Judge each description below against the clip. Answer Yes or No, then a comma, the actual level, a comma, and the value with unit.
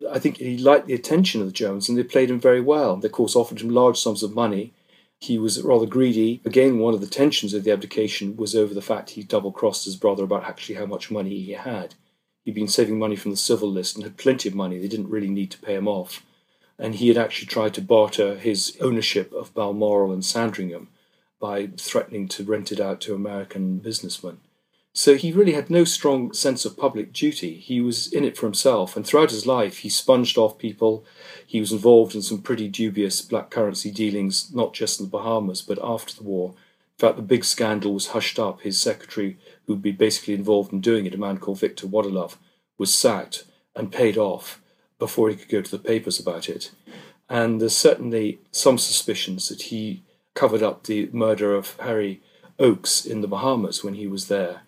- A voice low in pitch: Yes, low, 110 Hz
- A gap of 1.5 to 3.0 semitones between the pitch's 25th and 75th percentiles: Yes, average, 2.7 semitones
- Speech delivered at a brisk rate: Yes, fast, 215 wpm